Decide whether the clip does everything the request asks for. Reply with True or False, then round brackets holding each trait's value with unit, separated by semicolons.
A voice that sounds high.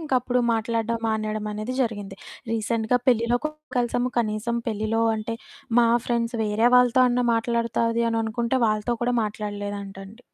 True (230 Hz)